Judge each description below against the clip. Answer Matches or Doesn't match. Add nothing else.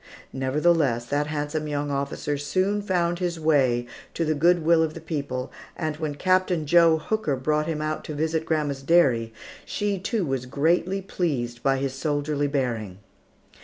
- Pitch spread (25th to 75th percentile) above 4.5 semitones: Doesn't match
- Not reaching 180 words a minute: Matches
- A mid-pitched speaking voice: Matches